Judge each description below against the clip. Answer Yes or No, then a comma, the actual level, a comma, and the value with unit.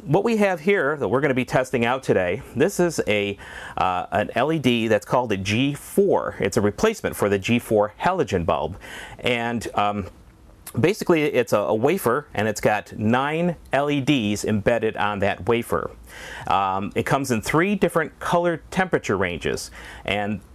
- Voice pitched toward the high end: No, low, 120 Hz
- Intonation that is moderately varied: No, wide, 6.2 semitones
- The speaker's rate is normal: Yes, average, 165 wpm